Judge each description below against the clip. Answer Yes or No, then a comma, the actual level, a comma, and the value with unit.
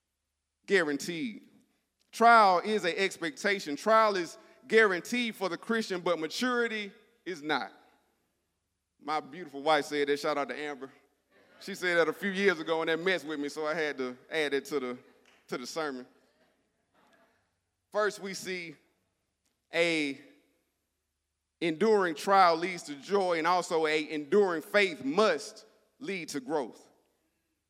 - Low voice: No, medium, 170 Hz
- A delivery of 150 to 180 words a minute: No, average, 140 wpm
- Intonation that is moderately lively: No, wide, 6.2 semitones